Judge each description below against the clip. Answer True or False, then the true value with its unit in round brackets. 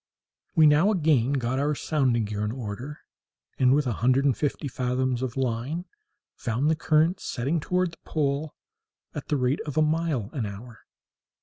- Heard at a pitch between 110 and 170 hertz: True (135 Hz)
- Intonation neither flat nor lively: True (3.8 semitones)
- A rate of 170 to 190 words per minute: True (175 wpm)